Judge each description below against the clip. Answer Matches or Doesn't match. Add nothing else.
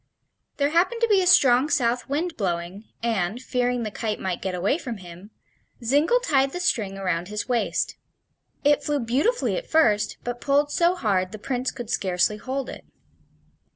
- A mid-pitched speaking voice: Doesn't match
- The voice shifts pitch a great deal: Matches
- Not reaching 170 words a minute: Doesn't match